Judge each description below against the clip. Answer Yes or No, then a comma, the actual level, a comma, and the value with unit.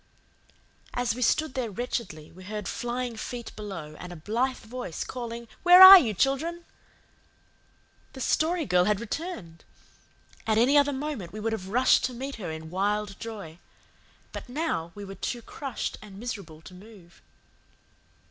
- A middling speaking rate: Yes, average, 155 wpm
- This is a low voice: No, high, 225 Hz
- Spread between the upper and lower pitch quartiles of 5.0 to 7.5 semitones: Yes, average, 5.3 semitones